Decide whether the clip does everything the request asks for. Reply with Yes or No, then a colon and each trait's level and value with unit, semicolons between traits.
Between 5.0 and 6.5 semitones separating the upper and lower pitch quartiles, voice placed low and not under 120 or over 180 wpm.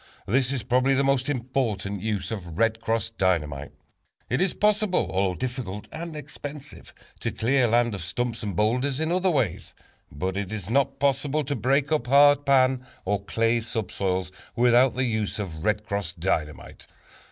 Yes: wide, 5.4 semitones; low, 120 Hz; average, 165 wpm